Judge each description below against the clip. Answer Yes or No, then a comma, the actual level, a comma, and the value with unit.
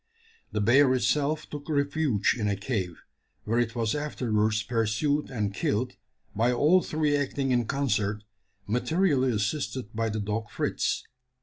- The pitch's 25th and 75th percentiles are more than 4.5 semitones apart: Yes, average, 5.0 semitones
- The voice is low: Yes, low, 120 Hz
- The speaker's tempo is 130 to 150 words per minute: Yes, average, 140 wpm